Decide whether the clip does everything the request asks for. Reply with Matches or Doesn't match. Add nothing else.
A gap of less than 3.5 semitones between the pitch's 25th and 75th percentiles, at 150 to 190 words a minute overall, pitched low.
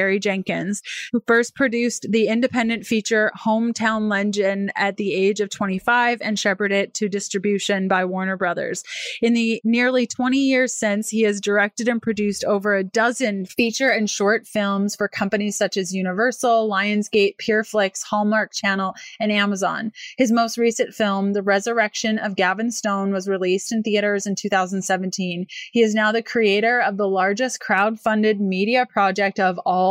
Doesn't match